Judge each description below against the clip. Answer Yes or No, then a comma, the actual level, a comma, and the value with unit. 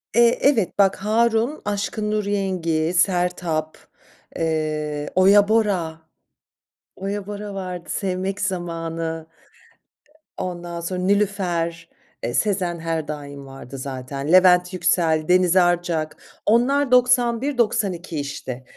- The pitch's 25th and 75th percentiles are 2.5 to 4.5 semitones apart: Yes, average, 3.9 semitones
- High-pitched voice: No, medium, 180 Hz